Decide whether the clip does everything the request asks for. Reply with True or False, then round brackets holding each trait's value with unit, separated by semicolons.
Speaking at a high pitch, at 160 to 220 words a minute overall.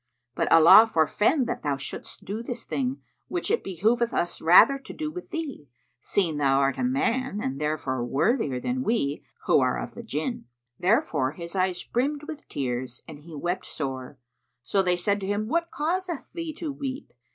True (200 Hz; 185 wpm)